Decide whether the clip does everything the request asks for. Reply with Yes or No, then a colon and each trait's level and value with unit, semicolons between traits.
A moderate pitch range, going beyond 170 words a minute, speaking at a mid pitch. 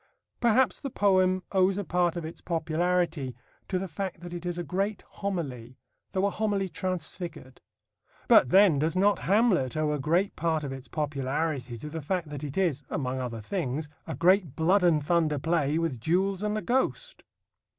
Yes: average, 4.4 semitones; average, 180 wpm; medium, 170 Hz